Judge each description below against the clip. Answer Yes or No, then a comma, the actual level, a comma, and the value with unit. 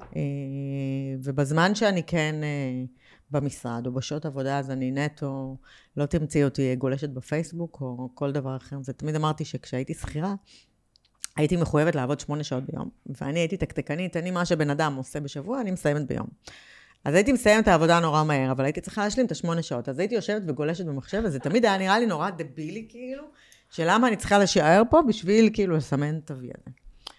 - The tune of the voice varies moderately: Yes, average, 4.9 semitones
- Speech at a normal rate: No, fast, 180 wpm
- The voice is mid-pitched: Yes, medium, 150 Hz